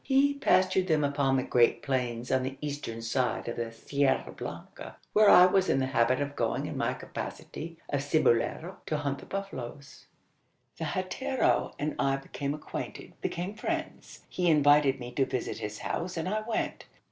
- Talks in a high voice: No, medium, 145 Hz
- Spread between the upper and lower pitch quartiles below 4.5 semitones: No, wide, 5.5 semitones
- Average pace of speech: Yes, average, 175 wpm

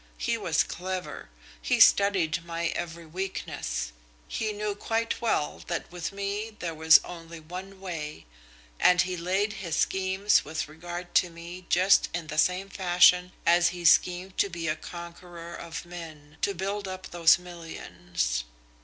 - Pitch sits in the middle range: Yes, medium, 175 Hz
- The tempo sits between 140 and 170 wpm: Yes, average, 155 wpm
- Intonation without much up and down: Yes, narrow, 2.3 semitones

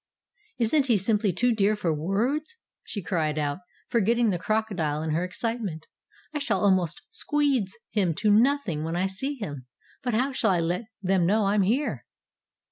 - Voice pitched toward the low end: No, high, 205 Hz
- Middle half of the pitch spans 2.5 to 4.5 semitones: No, average, 5.3 semitones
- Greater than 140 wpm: Yes, average, 170 wpm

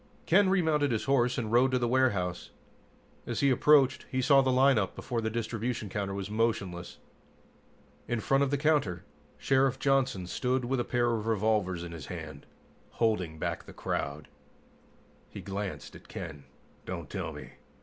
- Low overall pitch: Yes, low, 120 Hz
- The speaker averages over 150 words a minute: Yes, average, 170 wpm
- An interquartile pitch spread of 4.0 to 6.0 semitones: Yes, average, 5.1 semitones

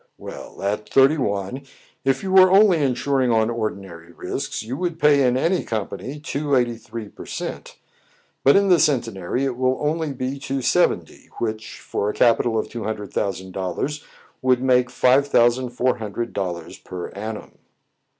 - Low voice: Yes, low, 125 Hz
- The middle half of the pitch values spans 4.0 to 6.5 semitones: Yes, average, 4.4 semitones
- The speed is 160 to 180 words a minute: Yes, average, 170 wpm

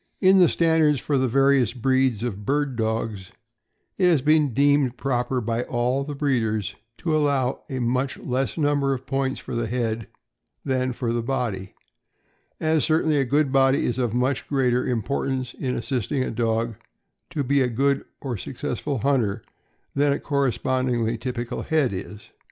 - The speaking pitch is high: No, low, 130 Hz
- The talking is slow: No, average, 165 wpm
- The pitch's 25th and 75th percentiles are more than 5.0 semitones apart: No, average, 2.8 semitones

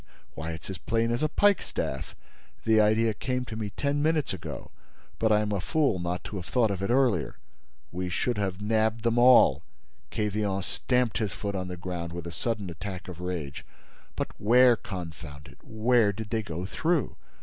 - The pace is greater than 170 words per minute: Yes, average, 180 wpm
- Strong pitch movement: No, average, 4.6 semitones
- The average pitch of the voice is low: Yes, low, 105 Hz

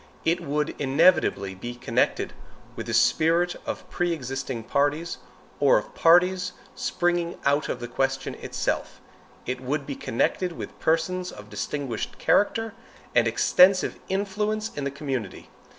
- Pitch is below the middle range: No, medium, 150 Hz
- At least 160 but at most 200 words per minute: No, slow, 135 wpm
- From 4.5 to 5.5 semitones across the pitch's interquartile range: Yes, average, 5.1 semitones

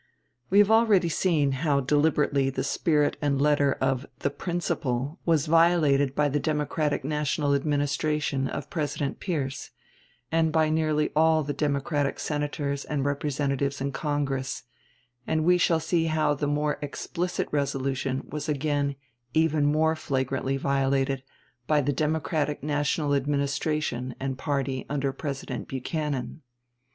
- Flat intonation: Yes, narrow, 2.0 semitones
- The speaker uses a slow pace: Yes, slow, 130 wpm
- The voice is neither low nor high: Yes, medium, 145 Hz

